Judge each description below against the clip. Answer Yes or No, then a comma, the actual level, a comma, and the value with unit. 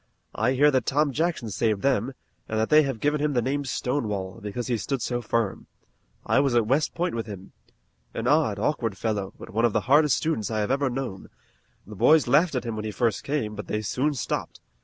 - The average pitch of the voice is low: Yes, low, 120 Hz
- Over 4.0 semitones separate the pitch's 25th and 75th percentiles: Yes, average, 4.8 semitones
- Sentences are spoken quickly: Yes, fast, 220 wpm